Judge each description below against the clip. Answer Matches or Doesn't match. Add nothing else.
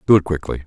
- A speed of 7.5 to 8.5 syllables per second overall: Matches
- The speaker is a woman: Doesn't match